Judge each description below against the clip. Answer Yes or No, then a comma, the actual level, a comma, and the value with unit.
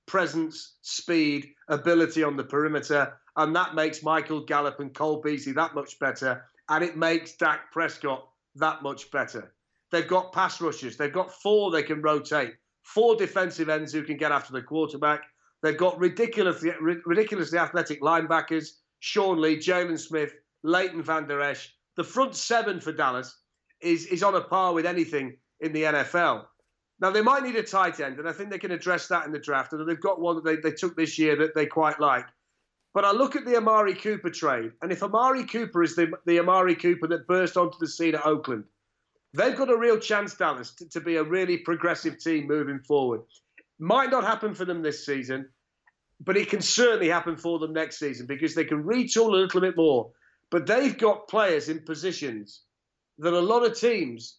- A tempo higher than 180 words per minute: Yes, average, 195 wpm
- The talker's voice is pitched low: No, medium, 165 Hz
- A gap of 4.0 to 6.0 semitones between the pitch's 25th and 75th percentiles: No, average, 3.4 semitones